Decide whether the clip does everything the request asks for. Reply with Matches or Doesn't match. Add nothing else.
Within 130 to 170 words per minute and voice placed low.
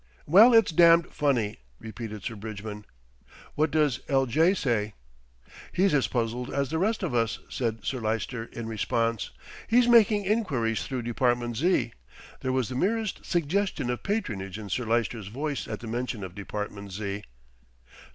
Matches